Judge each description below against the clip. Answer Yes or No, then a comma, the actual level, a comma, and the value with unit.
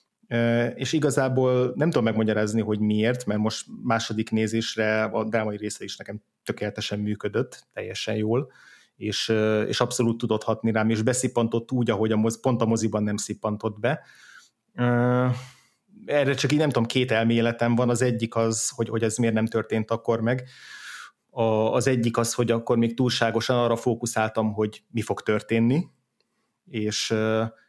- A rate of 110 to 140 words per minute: No, fast, 155 wpm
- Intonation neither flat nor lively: No, narrow, 2.0 semitones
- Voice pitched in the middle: No, low, 115 Hz